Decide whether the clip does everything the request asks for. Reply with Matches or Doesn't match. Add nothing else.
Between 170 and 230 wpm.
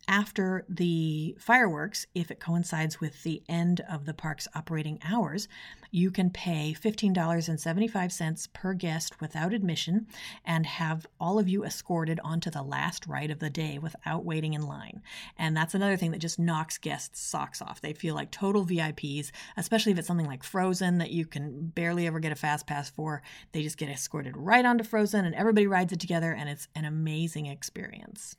Matches